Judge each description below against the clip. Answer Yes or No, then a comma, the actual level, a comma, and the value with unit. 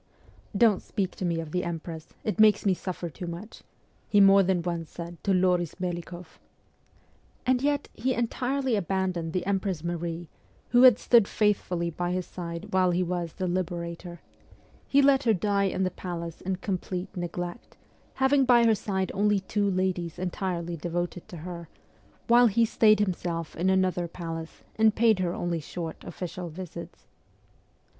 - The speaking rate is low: No, average, 165 wpm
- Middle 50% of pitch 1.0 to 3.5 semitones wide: Yes, average, 3.2 semitones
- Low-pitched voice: No, medium, 185 Hz